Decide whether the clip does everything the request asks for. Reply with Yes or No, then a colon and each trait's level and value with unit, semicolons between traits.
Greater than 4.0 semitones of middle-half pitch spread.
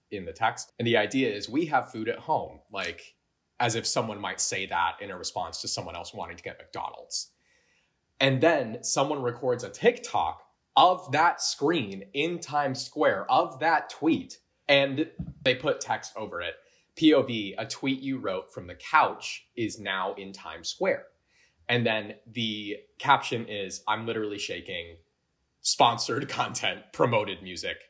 Yes: average, 4.6 semitones